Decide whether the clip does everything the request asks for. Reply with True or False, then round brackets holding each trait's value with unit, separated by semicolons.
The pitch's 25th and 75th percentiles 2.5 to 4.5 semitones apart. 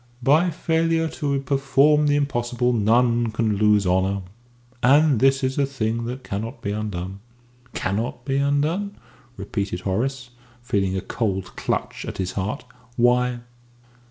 False (5.1 semitones)